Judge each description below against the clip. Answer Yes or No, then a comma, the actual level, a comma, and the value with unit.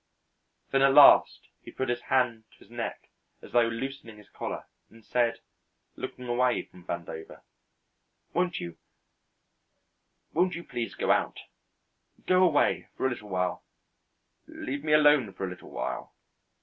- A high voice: No, low, 120 Hz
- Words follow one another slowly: No, average, 150 wpm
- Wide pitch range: No, average, 4.0 semitones